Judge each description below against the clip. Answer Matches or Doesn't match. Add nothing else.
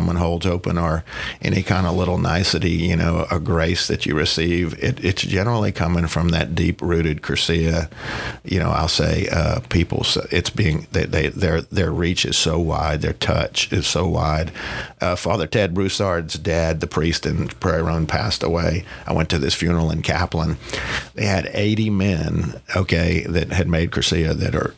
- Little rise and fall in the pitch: Matches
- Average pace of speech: Matches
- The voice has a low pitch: Matches